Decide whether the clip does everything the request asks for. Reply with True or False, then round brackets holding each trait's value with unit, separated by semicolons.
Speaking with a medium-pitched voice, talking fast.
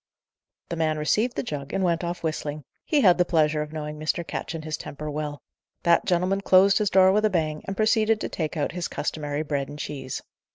True (160 Hz; 220 wpm)